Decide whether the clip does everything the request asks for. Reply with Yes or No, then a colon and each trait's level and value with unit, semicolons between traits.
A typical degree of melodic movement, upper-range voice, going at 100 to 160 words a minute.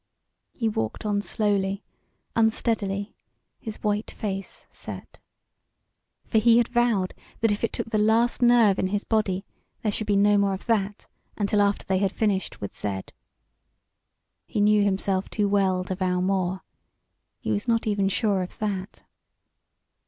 No: narrow, 2.1 semitones; high, 205 Hz; average, 155 wpm